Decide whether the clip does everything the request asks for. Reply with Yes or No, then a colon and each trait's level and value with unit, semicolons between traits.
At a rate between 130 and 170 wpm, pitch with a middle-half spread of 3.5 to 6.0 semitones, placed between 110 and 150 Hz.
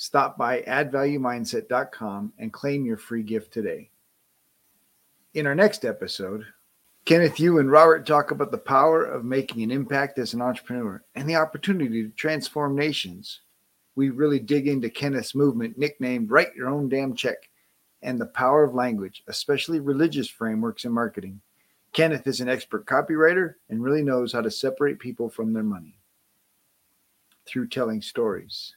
Yes: average, 155 wpm; average, 3.9 semitones; medium, 140 Hz